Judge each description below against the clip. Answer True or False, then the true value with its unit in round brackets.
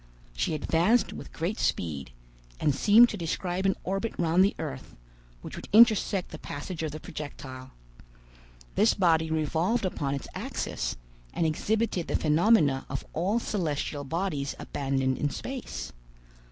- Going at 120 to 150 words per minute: True (140 wpm)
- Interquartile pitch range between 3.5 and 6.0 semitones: True (5.3 semitones)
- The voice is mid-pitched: True (165 Hz)